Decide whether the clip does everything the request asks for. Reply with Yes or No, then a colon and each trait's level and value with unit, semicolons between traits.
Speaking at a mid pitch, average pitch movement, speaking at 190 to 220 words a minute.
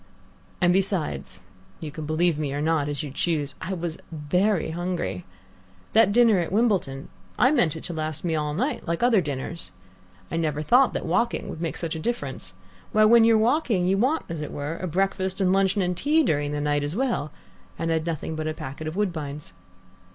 Yes: medium, 170 Hz; average, 4.5 semitones; average, 200 wpm